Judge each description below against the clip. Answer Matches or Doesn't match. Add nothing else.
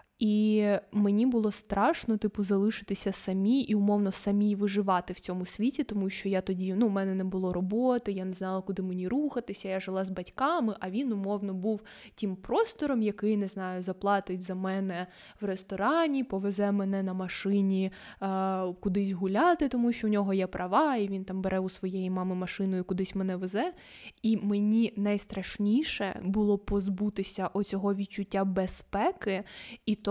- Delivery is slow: Doesn't match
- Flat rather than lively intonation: Matches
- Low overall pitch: Doesn't match